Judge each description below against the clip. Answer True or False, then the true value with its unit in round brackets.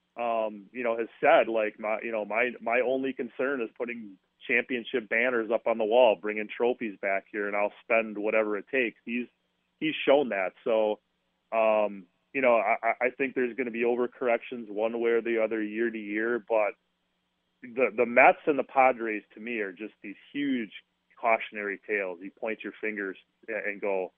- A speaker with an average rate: True (190 wpm)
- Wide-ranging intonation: False (2.4 semitones)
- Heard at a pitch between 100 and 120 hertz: True (115 Hz)